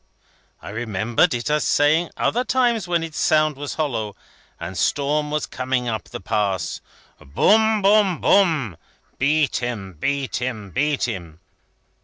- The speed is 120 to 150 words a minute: Yes, average, 140 wpm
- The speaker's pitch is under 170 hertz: Yes, medium, 140 Hz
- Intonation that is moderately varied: No, wide, 6.6 semitones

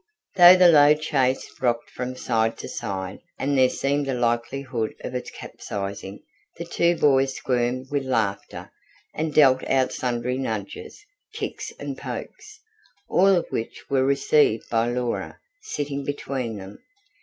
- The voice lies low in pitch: Yes, low, 130 Hz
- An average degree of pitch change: Yes, average, 3.5 semitones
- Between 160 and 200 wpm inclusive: No, average, 145 wpm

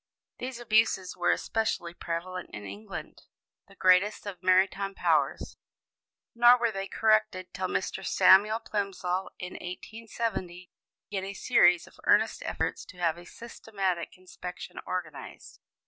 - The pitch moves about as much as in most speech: Yes, average, 3.3 semitones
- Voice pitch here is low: No, high, 190 Hz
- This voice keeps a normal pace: No, slow, 130 wpm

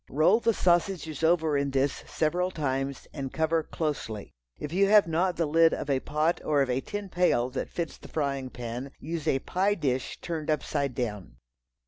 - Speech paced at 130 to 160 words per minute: No, average, 185 wpm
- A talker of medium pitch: Yes, medium, 155 Hz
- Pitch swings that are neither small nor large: Yes, average, 3.9 semitones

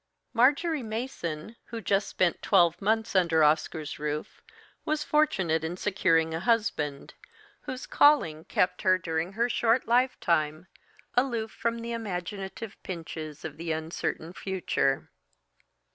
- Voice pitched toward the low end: No, medium, 185 Hz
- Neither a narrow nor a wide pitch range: No, wide, 6.2 semitones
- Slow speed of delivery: Yes, slow, 125 wpm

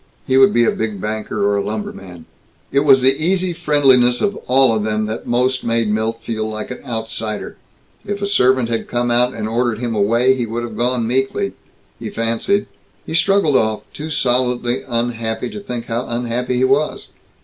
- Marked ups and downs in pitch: No, average, 2.8 semitones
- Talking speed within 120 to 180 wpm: No, average, 190 wpm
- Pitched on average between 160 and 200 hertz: No, low, 120 Hz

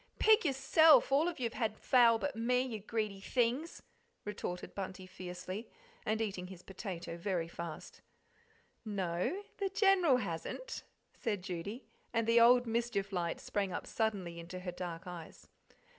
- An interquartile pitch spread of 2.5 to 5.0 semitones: No, wide, 5.4 semitones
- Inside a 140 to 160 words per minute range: Yes, average, 150 wpm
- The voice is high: Yes, high, 215 Hz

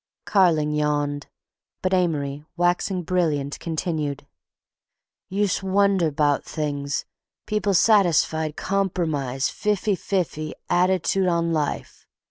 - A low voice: No, medium, 170 Hz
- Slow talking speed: Yes, slow, 90 wpm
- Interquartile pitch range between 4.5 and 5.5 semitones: No, average, 4.1 semitones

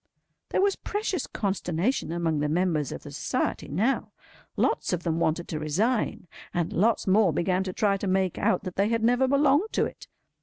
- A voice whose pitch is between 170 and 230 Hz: Yes, high, 190 Hz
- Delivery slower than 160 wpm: No, average, 190 wpm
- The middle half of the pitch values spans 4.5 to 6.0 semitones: Yes, wide, 5.4 semitones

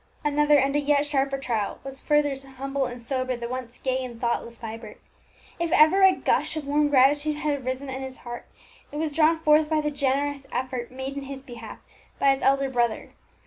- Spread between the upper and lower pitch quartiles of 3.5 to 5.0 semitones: No, narrow, 2.4 semitones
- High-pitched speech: Yes, very high, 275 Hz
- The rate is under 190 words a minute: No, fast, 205 wpm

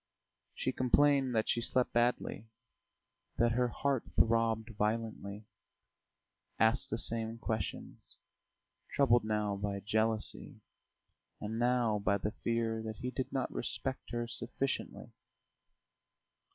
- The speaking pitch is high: No, low, 115 Hz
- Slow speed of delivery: Yes, slow, 110 wpm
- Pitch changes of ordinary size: No, narrow, 2.2 semitones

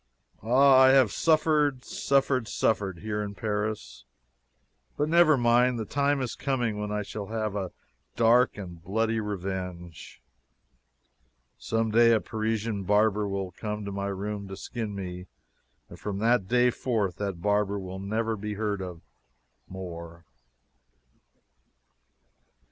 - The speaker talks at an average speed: No, slow, 130 wpm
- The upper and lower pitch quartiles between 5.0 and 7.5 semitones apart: No, average, 3.2 semitones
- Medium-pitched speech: No, low, 105 Hz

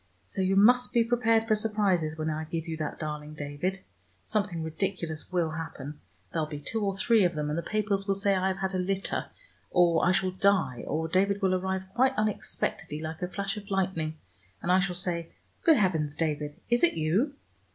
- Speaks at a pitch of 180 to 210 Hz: Yes, medium, 185 Hz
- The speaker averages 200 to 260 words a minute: Yes, fast, 205 wpm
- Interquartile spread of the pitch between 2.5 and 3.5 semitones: No, average, 4.1 semitones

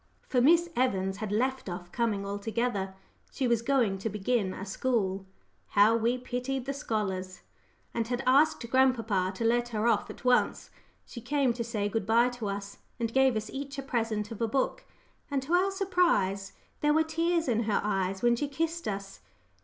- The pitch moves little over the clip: No, average, 4.6 semitones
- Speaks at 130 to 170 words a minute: No, average, 185 wpm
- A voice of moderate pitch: No, high, 235 Hz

